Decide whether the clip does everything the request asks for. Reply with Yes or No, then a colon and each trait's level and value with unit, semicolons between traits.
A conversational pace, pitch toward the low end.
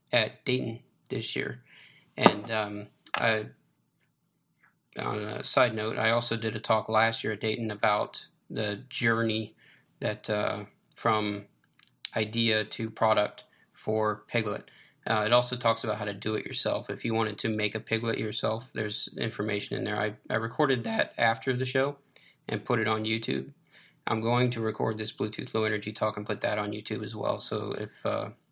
Yes: average, 175 wpm; low, 110 Hz